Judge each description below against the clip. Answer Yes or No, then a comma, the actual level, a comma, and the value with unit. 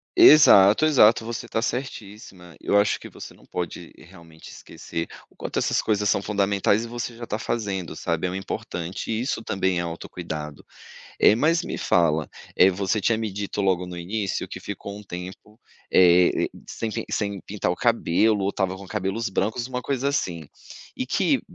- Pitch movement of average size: Yes, average, 3.9 semitones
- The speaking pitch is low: Yes, low, 100 Hz